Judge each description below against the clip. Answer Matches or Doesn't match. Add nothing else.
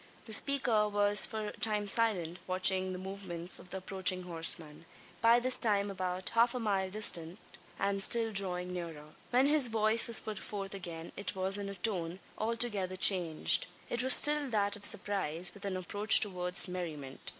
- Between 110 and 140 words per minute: Doesn't match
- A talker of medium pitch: Doesn't match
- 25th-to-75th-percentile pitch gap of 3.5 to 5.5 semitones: Doesn't match